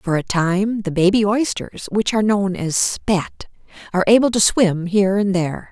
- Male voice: No, female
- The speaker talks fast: No, average, 170 wpm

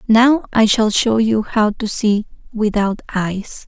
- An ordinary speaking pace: Yes, average, 165 wpm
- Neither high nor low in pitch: No, high, 220 Hz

